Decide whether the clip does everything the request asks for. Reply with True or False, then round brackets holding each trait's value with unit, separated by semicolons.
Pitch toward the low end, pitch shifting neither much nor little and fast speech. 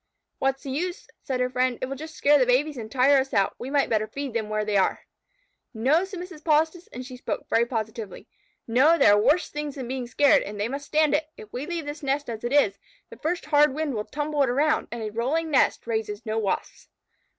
False (270 Hz; 4.5 semitones; 240 wpm)